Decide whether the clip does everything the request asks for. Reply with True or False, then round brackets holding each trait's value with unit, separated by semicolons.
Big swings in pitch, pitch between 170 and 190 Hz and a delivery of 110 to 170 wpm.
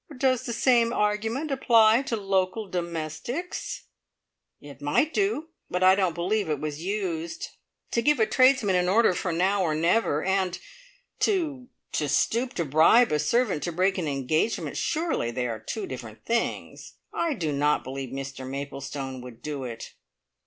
True (7.8 semitones; 185 Hz; 160 wpm)